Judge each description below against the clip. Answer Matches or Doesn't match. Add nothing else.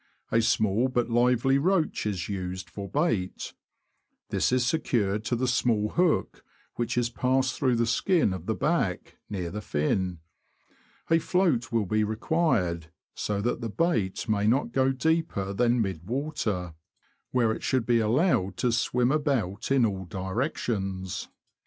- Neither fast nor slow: Matches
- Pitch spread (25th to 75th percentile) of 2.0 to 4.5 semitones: Doesn't match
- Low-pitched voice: Matches